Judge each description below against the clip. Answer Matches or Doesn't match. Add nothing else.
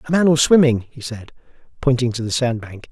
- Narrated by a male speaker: Matches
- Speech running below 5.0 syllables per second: Doesn't match